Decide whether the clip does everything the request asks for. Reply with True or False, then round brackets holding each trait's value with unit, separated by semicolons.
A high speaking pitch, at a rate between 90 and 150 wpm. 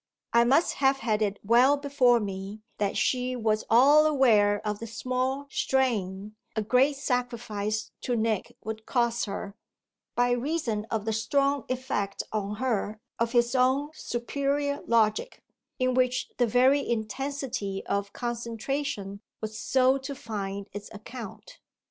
True (235 Hz; 140 wpm)